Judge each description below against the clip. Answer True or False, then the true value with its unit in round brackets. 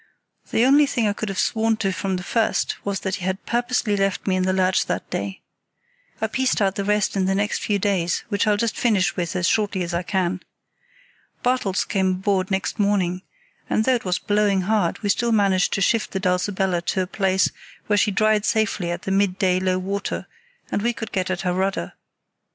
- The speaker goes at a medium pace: False (215 wpm)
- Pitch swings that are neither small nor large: False (2.3 semitones)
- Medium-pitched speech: False (195 Hz)